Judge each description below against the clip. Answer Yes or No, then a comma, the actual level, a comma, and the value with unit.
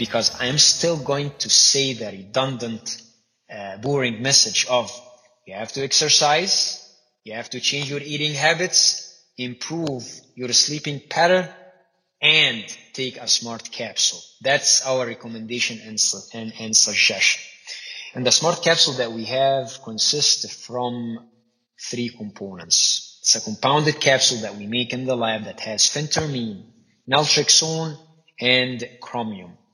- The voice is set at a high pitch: No, low, 125 Hz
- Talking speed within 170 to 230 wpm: No, slow, 135 wpm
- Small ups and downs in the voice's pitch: No, average, 3.8 semitones